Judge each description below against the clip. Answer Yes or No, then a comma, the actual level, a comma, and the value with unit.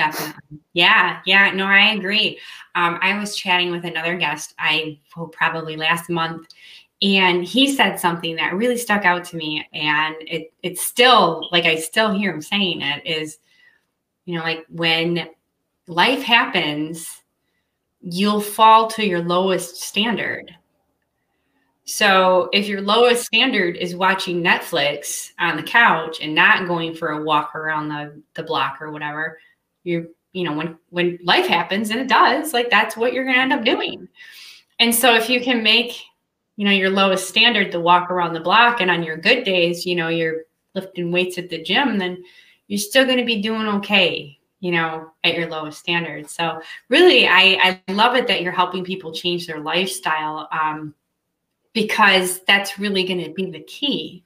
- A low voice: No, medium, 180 Hz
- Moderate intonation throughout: Yes, average, 4.0 semitones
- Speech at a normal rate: Yes, average, 175 wpm